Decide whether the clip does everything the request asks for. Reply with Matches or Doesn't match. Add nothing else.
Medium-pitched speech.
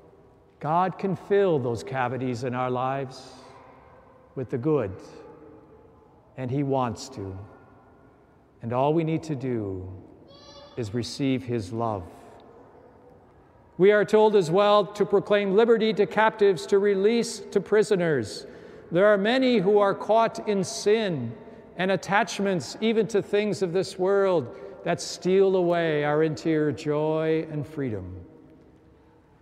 Matches